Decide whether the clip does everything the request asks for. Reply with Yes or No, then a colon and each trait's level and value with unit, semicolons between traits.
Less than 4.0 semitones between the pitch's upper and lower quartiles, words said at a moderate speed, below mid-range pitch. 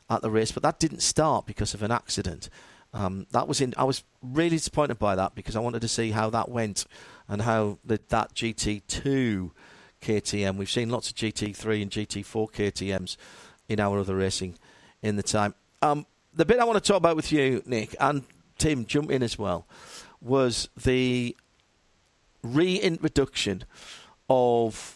No: average, 4.5 semitones; average, 170 wpm; low, 110 Hz